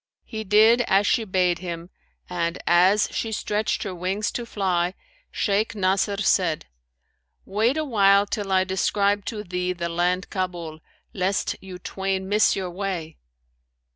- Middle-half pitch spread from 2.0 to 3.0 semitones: Yes, narrow, 2.4 semitones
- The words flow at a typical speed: Yes, average, 145 wpm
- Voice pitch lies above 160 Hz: Yes, high, 190 Hz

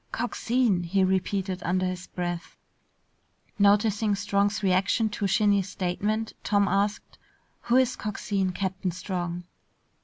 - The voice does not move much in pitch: Yes, narrow, 2.2 semitones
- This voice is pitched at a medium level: No, high, 200 Hz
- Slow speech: Yes, slow, 115 wpm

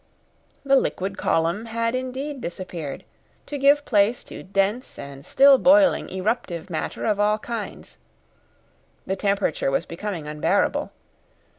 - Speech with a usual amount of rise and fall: No, wide, 6.5 semitones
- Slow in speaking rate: Yes, slow, 125 wpm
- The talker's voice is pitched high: Yes, high, 205 Hz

